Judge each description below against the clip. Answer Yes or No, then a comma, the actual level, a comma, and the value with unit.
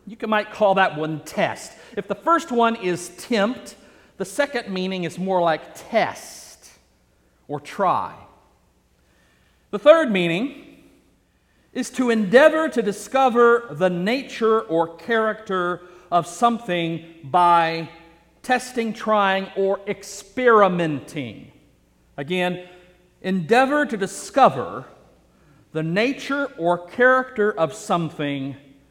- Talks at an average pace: No, slow, 105 wpm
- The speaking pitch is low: No, high, 190 Hz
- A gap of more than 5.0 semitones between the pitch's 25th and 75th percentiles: Yes, wide, 5.6 semitones